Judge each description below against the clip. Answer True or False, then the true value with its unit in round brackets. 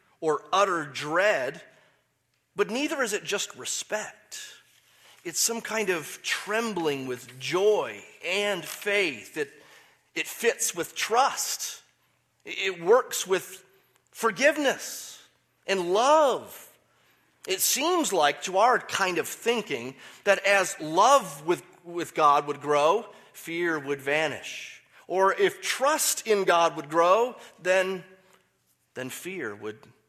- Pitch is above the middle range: True (195 Hz)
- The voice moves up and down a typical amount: False (8.0 semitones)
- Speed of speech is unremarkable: False (120 wpm)